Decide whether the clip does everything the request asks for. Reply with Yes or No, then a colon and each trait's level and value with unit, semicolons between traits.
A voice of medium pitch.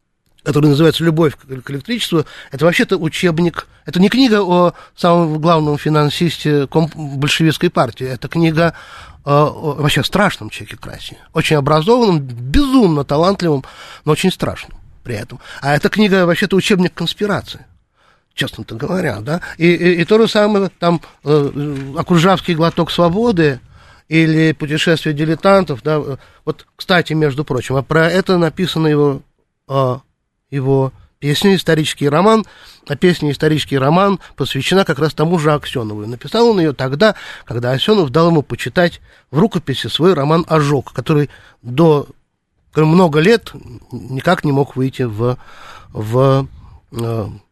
Yes: medium, 155 Hz